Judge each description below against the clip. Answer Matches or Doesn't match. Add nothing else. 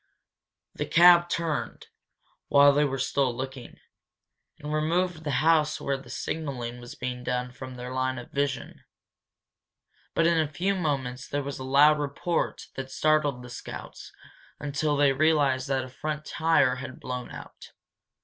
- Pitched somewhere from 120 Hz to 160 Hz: Matches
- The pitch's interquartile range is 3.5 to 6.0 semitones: Doesn't match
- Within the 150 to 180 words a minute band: Matches